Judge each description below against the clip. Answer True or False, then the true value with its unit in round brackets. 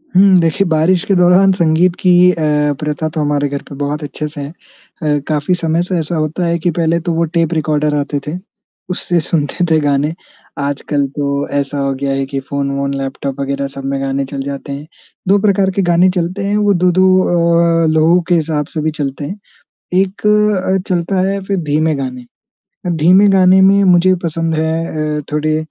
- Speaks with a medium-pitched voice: True (160 Hz)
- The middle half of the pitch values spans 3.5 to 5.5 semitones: True (3.9 semitones)